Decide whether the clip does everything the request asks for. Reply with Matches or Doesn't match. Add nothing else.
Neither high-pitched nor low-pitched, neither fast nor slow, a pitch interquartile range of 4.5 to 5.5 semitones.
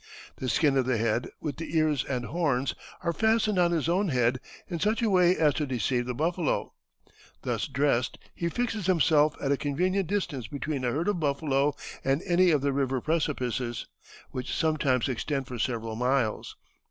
Matches